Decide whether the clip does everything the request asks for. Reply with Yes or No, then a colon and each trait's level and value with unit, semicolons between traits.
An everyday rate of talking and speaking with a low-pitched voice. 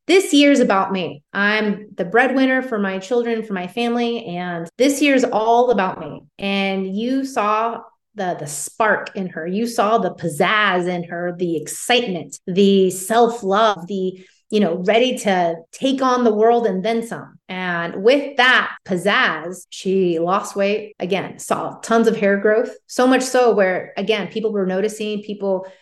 No: average, 165 wpm; high, 205 Hz